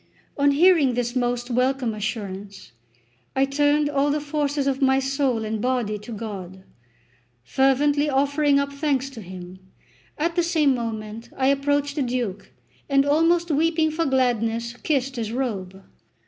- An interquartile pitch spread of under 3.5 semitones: No, average, 4.1 semitones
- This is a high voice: Yes, very high, 265 Hz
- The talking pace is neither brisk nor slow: Yes, average, 150 wpm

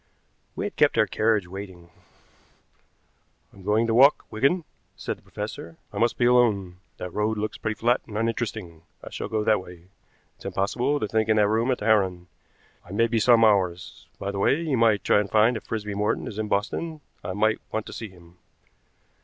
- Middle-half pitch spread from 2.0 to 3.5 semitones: Yes, average, 2.8 semitones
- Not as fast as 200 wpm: No, fast, 205 wpm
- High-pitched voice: No, low, 110 Hz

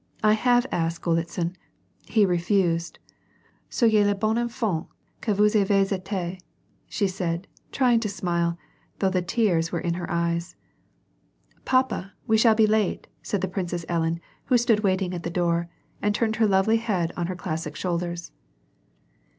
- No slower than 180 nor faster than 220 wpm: No, average, 160 wpm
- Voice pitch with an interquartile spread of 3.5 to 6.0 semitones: Yes, average, 3.9 semitones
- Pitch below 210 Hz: Yes, high, 190 Hz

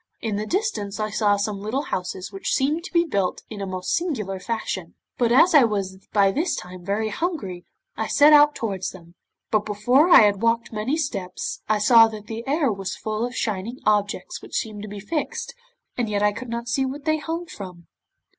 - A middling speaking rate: No, fast, 210 wpm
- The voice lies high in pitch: Yes, high, 215 Hz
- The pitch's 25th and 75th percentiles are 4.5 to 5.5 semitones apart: Yes, average, 5.1 semitones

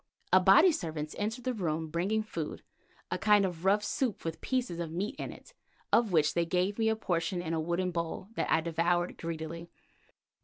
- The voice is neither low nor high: Yes, medium, 175 Hz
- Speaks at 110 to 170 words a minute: No, average, 190 wpm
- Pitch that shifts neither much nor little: Yes, average, 4.1 semitones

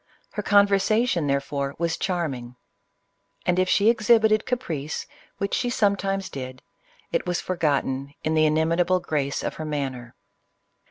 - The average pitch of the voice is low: No, medium, 170 Hz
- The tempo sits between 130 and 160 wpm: Yes, average, 140 wpm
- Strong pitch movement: Yes, wide, 5.9 semitones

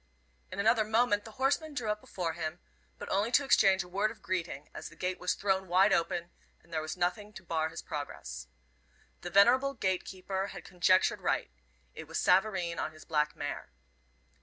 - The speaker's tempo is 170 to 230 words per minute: Yes, average, 190 wpm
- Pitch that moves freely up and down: No, average, 3.9 semitones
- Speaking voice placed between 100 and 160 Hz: No, medium, 185 Hz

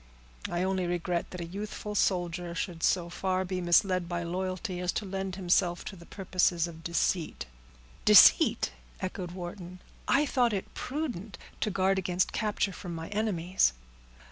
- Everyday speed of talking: Yes, average, 155 wpm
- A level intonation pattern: Yes, narrow, 1.9 semitones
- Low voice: No, medium, 185 Hz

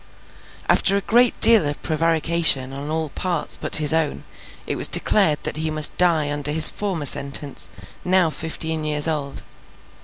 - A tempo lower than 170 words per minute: Yes, average, 160 wpm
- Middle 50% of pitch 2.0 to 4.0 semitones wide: Yes, narrow, 2.4 semitones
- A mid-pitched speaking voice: Yes, medium, 155 Hz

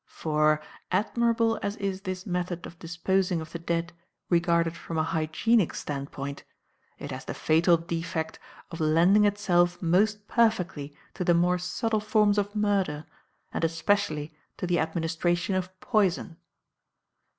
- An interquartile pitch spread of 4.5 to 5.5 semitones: No, average, 3.7 semitones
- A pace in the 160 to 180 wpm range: No, average, 140 wpm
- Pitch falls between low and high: Yes, medium, 175 Hz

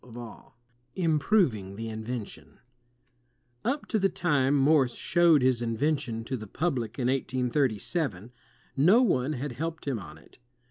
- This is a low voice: Yes, low, 130 Hz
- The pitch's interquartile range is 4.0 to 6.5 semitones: Yes, average, 5.3 semitones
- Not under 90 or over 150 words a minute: Yes, average, 140 wpm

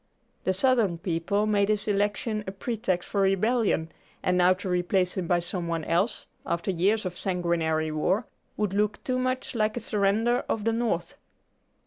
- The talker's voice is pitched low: No, high, 195 Hz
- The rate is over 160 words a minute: Yes, average, 170 wpm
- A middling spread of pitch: Yes, average, 3.3 semitones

